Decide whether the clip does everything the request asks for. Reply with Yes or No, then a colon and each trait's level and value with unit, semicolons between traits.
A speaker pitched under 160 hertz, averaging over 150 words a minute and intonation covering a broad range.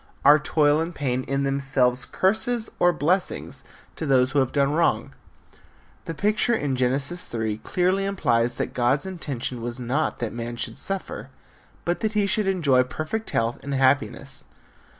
Yes: medium, 140 Hz; average, 160 wpm; wide, 5.7 semitones